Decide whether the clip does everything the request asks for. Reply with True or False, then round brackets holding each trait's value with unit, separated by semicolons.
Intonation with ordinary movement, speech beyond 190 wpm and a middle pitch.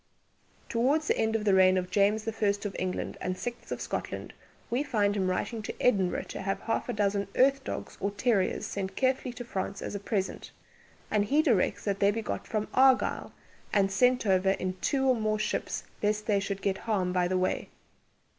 False (3.1 semitones; 205 wpm; 205 Hz)